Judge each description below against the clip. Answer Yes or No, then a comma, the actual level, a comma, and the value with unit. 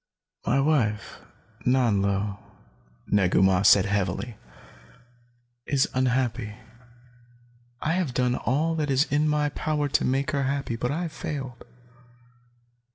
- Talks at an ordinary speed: No, slow, 120 wpm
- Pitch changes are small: No, wide, 5.5 semitones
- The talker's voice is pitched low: Yes, low, 130 Hz